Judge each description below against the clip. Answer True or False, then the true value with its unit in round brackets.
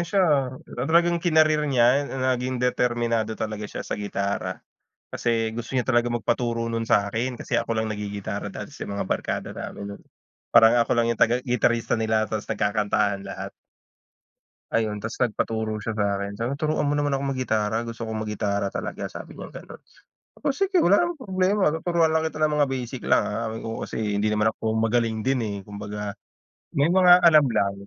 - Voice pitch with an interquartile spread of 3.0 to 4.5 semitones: False (4.9 semitones)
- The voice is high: False (115 Hz)